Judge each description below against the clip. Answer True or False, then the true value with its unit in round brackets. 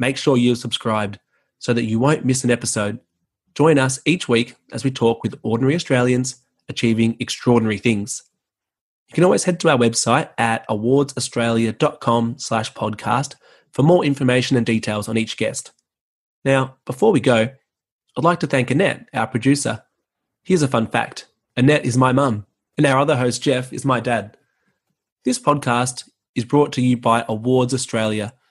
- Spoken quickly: False (160 wpm)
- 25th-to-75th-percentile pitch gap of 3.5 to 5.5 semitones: False (2.8 semitones)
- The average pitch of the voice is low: True (125 Hz)